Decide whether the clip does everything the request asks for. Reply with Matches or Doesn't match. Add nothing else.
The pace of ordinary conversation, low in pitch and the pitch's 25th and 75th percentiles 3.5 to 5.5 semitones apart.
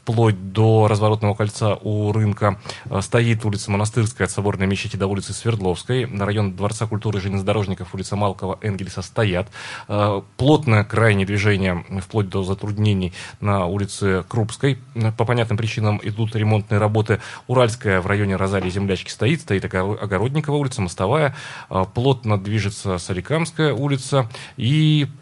Doesn't match